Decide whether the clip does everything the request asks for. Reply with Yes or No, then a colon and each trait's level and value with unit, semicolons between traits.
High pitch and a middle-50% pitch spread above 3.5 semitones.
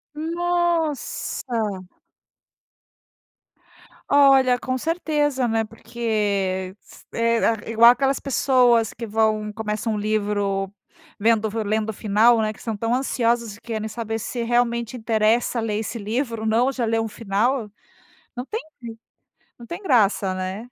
No: high, 230 Hz; average, 2.7 semitones